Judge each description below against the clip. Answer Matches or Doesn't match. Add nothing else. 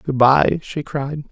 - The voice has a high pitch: Doesn't match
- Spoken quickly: Doesn't match